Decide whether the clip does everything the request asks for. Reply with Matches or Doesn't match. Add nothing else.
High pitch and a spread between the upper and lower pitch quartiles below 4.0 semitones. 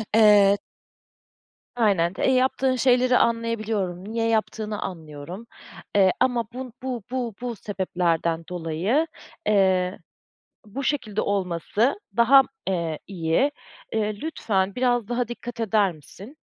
Doesn't match